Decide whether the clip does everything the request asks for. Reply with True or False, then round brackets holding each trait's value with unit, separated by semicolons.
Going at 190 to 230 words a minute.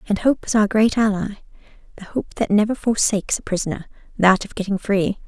False (170 wpm)